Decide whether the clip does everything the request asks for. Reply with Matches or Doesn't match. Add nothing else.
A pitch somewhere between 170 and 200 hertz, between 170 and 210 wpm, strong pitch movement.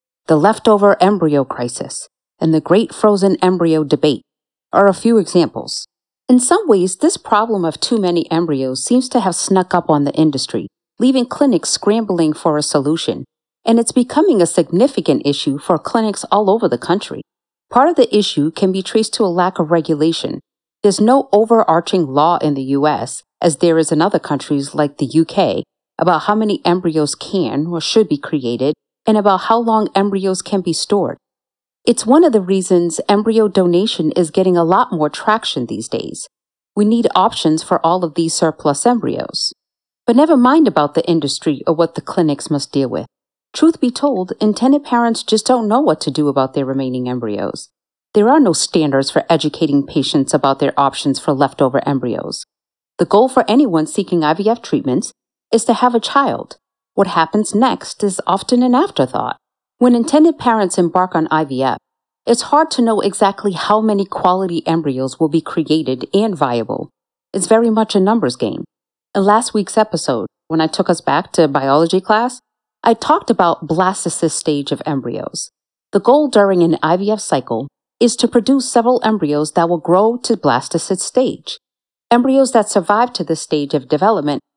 Matches